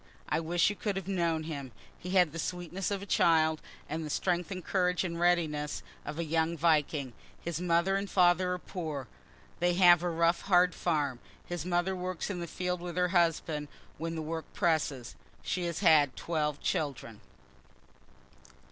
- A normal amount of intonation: No, narrow, 2.3 semitones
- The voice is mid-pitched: Yes, medium, 170 Hz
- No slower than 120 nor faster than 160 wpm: No, average, 175 wpm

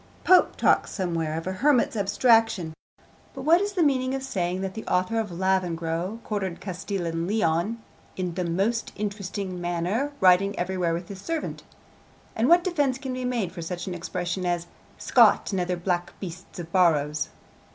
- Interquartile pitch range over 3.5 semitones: Yes, average, 4.4 semitones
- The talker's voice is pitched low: No, high, 190 Hz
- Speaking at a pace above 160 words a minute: Yes, average, 170 wpm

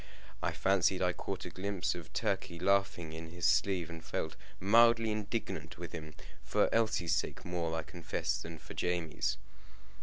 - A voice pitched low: Yes, very low, 90 Hz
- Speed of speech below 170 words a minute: Yes, average, 160 wpm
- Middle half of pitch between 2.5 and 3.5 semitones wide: Yes, average, 3.2 semitones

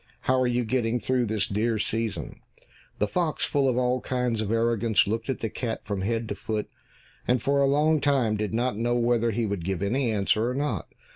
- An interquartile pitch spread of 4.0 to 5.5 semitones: No, average, 2.8 semitones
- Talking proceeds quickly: Yes, fast, 215 wpm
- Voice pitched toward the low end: Yes, low, 115 Hz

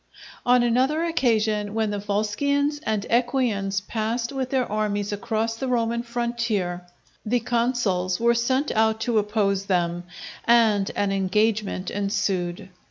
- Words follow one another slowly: Yes, slow, 130 wpm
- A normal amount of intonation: Yes, average, 3.0 semitones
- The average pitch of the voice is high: Yes, high, 220 Hz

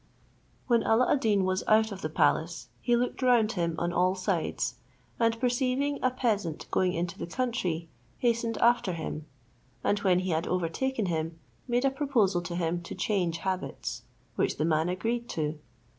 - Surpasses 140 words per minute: Yes, average, 175 wpm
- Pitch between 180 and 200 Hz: Yes, high, 190 Hz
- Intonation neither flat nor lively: No, wide, 5.8 semitones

